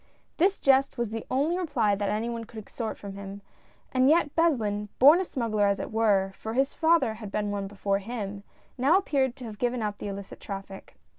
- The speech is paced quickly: Yes, fast, 220 wpm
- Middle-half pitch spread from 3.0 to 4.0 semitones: No, average, 4.8 semitones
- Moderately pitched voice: No, high, 225 Hz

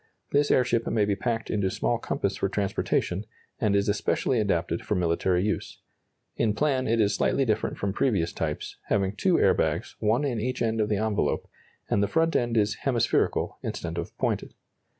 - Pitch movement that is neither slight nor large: Yes, average, 3.3 semitones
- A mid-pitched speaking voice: No, low, 105 Hz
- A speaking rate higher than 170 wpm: Yes, average, 185 wpm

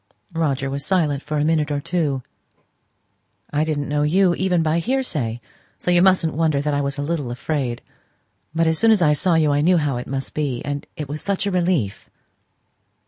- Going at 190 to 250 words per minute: Yes, average, 200 wpm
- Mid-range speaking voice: Yes, medium, 150 Hz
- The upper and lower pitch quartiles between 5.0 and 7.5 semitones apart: No, average, 3.3 semitones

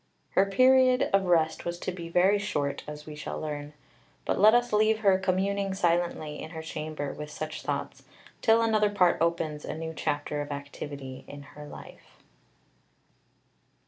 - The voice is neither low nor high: Yes, medium, 170 Hz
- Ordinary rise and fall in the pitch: Yes, average, 5.0 semitones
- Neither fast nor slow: Yes, average, 165 wpm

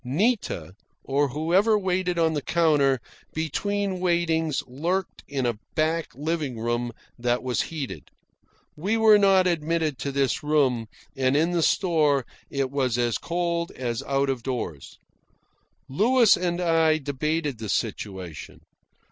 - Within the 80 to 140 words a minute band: Yes, slow, 135 wpm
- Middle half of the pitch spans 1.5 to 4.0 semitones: No, average, 4.9 semitones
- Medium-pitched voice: Yes, medium, 150 Hz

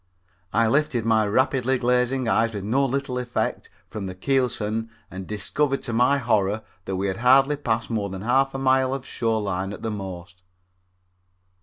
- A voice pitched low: Yes, low, 115 Hz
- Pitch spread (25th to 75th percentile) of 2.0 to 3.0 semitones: No, average, 4.2 semitones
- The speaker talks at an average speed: Yes, average, 175 wpm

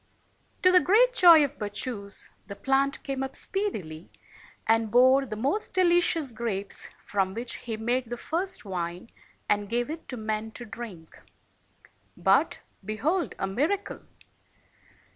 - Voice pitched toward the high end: Yes, high, 240 Hz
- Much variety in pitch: Yes, wide, 6.9 semitones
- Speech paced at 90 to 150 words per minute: Yes, average, 145 wpm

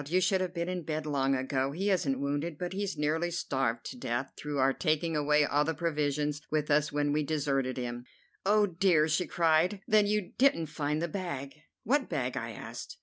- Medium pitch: Yes, medium, 150 Hz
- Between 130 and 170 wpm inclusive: No, fast, 205 wpm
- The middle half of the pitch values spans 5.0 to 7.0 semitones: No, average, 3.9 semitones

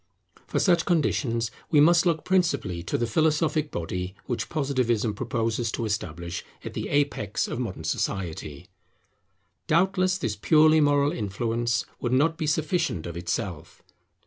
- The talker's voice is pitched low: Yes, low, 120 Hz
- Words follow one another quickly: No, average, 140 wpm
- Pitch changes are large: Yes, wide, 7.5 semitones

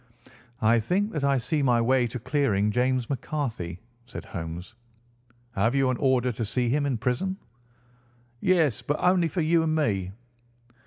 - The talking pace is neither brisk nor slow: Yes, average, 160 wpm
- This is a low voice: Yes, low, 130 Hz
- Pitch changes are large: No, average, 4.6 semitones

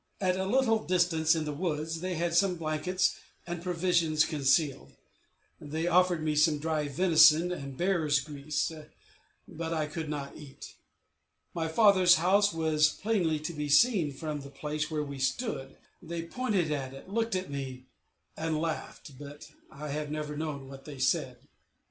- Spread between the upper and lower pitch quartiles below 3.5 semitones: Yes, average, 3.0 semitones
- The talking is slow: No, average, 160 wpm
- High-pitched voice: No, medium, 155 Hz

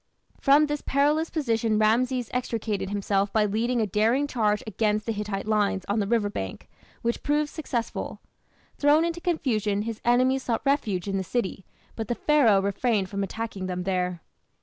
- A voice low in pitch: No, high, 220 Hz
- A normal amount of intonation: Yes, average, 4.1 semitones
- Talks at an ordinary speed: Yes, average, 170 wpm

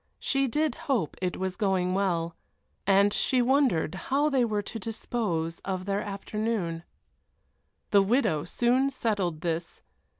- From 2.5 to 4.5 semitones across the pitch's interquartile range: No, average, 5.1 semitones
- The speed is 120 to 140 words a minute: Yes, slow, 135 wpm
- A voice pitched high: Yes, high, 200 Hz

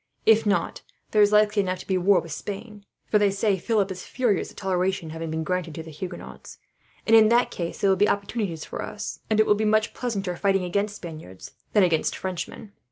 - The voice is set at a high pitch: Yes, high, 195 Hz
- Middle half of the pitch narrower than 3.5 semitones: Yes, average, 2.9 semitones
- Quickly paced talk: Yes, fast, 220 wpm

